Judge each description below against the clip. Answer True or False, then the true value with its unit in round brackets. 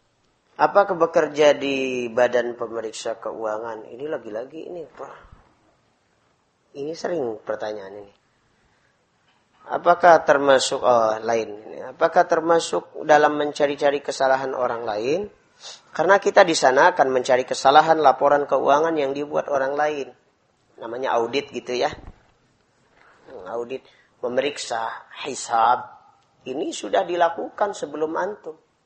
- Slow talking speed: True (100 wpm)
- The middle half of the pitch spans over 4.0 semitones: True (4.9 semitones)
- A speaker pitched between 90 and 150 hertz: True (140 Hz)